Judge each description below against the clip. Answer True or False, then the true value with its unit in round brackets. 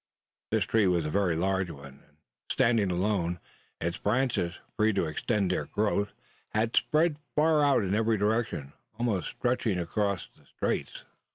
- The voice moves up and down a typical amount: True (4.4 semitones)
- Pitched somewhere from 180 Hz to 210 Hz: False (100 Hz)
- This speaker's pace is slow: False (155 wpm)